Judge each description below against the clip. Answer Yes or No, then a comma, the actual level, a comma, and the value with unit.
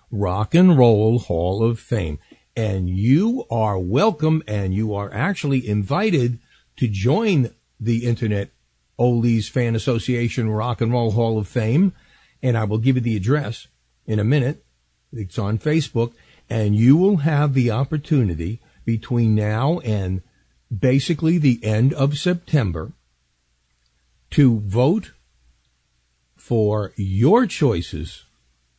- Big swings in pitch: Yes, wide, 5.8 semitones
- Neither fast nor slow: No, slow, 125 wpm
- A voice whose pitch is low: Yes, low, 115 Hz